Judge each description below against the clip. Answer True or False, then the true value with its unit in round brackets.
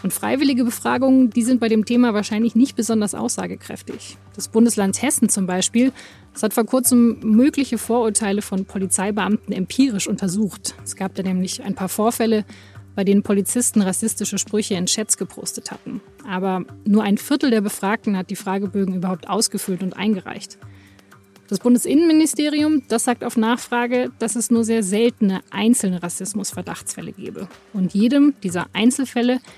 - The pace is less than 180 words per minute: True (150 wpm)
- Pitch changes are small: False (3.7 semitones)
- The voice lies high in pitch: True (215 Hz)